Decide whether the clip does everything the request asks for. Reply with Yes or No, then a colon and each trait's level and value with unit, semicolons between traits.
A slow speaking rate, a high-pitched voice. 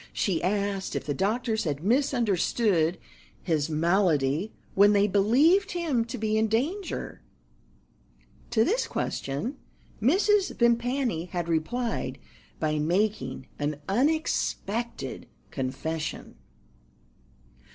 Yes: slow, 100 wpm; high, 205 Hz